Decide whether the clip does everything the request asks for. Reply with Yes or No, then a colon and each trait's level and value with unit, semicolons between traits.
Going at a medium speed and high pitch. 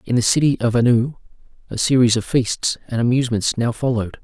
No: average, 185 wpm; low, 120 Hz